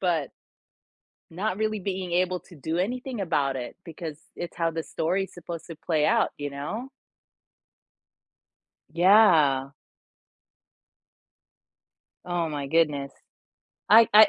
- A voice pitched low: No, medium, 170 Hz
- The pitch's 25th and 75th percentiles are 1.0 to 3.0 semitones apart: No, average, 4.3 semitones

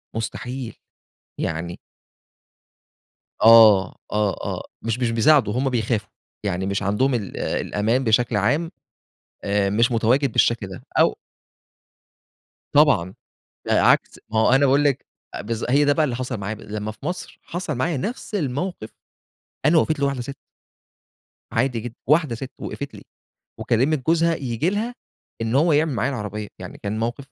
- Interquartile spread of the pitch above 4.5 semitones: Yes, average, 4.9 semitones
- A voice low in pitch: Yes, low, 125 Hz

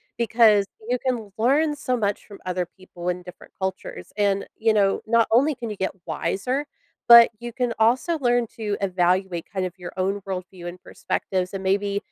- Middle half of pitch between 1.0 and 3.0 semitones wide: No, average, 3.9 semitones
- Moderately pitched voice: No, high, 205 Hz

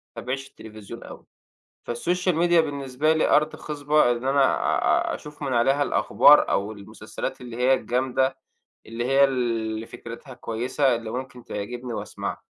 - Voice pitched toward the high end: No, low, 130 Hz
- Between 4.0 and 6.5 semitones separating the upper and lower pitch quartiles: No, average, 3.3 semitones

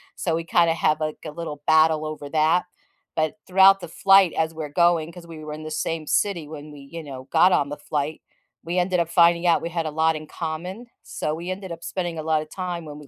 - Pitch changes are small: Yes, narrow, 2.1 semitones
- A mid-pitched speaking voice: Yes, medium, 160 Hz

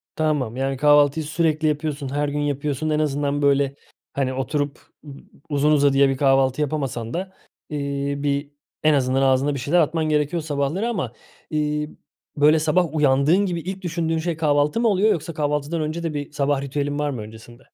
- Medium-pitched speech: Yes, medium, 145 Hz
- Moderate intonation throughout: No, narrow, 2.1 semitones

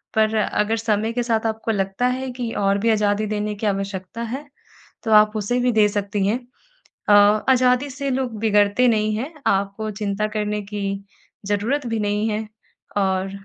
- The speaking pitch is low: No, high, 215 Hz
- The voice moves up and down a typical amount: No, narrow, 2.1 semitones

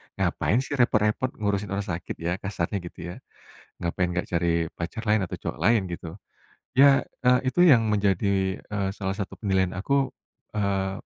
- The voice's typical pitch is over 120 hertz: No, low, 100 Hz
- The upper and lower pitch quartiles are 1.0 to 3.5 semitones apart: Yes, average, 2.7 semitones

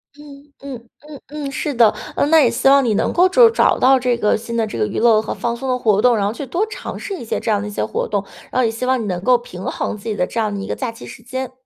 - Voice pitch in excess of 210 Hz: Yes, high, 245 Hz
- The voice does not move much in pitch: No, average, 4.2 semitones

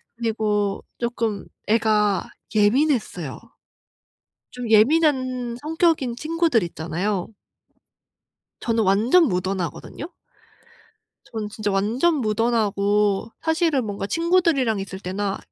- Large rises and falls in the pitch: No, average, 4.7 semitones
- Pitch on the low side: No, high, 220 Hz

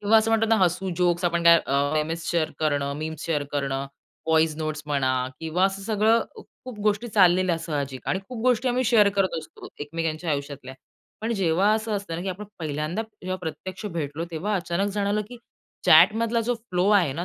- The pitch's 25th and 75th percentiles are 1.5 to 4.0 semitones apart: No, average, 5.0 semitones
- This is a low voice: No, medium, 175 Hz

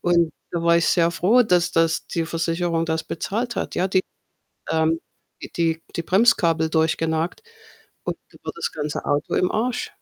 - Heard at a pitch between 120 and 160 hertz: No, medium, 170 Hz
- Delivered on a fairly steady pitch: Yes, narrow, 1.9 semitones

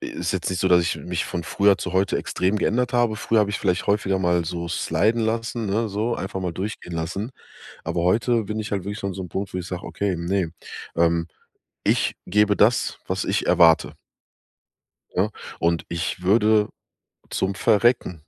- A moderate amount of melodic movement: Yes, average, 3.4 semitones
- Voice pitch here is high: No, very low, 95 Hz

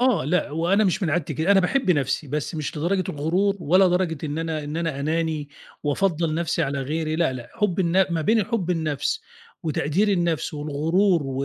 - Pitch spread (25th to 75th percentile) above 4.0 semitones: No, average, 3.6 semitones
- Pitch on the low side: No, medium, 165 Hz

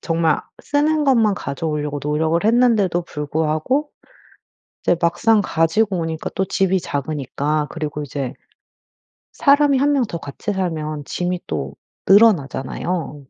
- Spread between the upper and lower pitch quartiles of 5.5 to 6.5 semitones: Yes, wide, 6.2 semitones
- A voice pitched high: No, medium, 170 Hz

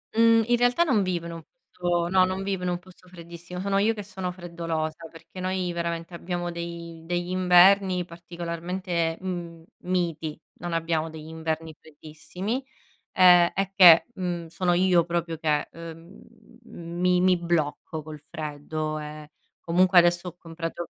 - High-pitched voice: No, medium, 175 Hz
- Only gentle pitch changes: Yes, narrow, 1.9 semitones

